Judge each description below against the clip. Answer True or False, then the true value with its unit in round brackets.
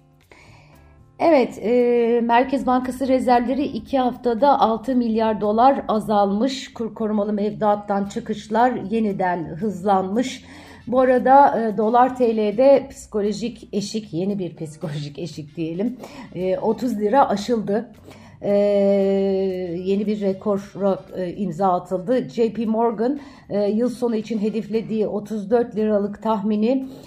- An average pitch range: True (3.4 semitones)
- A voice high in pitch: True (220 Hz)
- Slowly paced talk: False (110 wpm)